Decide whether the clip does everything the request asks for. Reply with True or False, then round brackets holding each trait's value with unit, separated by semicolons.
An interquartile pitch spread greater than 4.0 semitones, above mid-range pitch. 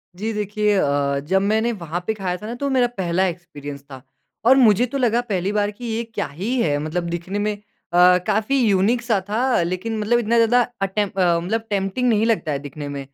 True (4.6 semitones; 205 Hz)